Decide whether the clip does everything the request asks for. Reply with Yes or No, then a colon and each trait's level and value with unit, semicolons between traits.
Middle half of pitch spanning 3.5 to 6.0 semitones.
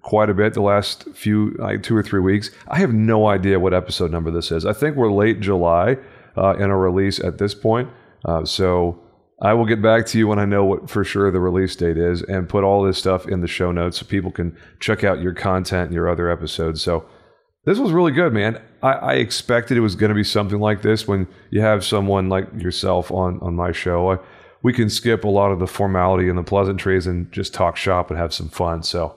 No: average, 2.8 semitones